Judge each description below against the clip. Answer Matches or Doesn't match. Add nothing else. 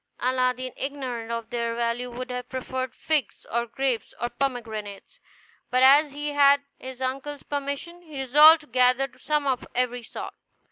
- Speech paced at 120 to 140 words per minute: Doesn't match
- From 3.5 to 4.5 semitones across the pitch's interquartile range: Doesn't match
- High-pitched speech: Matches